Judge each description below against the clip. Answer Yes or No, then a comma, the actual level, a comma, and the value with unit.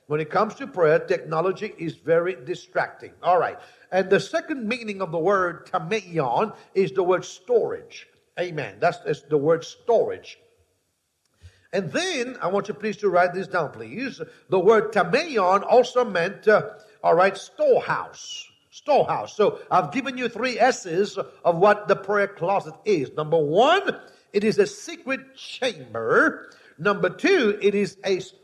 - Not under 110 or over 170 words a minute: Yes, average, 155 wpm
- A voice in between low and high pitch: No, high, 210 Hz